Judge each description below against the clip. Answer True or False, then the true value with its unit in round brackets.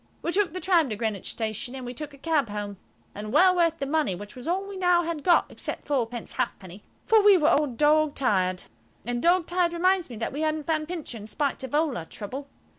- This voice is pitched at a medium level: False (295 Hz)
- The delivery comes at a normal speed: False (240 wpm)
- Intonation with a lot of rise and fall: True (6.8 semitones)